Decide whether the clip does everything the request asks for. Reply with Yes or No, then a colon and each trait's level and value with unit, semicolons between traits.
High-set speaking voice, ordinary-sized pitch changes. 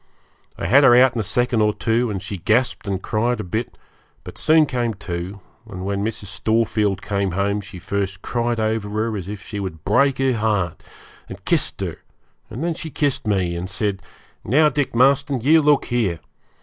No: low, 110 Hz; average, 3.9 semitones